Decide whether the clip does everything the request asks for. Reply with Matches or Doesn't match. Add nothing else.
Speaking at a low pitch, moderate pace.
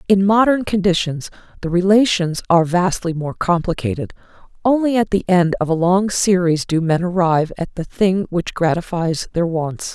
Doesn't match